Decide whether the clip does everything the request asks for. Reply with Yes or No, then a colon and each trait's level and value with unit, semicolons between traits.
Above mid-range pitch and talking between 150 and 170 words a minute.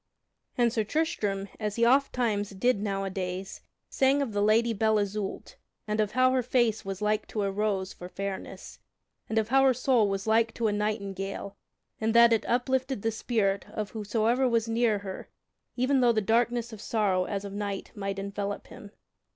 No: high, 215 Hz; average, 185 wpm